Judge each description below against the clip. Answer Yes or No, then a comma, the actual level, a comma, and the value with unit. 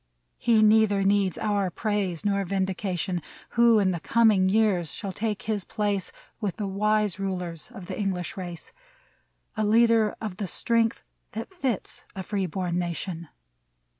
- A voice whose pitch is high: Yes, high, 200 Hz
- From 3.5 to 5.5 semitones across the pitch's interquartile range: No, average, 2.7 semitones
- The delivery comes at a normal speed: Yes, average, 155 wpm